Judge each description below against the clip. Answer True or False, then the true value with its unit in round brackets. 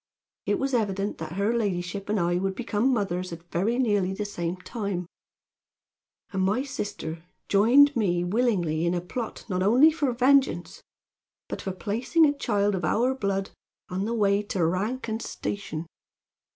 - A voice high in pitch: True (200 Hz)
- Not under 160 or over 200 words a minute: True (165 wpm)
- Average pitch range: True (4.6 semitones)